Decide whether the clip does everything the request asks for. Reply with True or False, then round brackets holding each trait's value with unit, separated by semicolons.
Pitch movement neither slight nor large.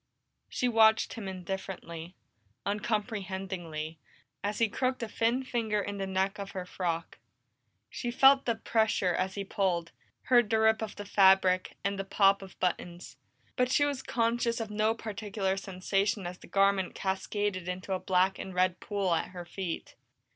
True (3.0 semitones)